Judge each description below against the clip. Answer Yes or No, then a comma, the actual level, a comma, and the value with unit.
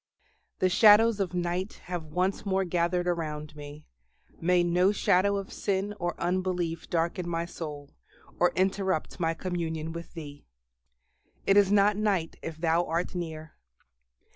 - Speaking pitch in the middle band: Yes, medium, 175 Hz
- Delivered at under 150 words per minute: Yes, average, 140 wpm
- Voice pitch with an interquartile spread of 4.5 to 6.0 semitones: No, narrow, 2.6 semitones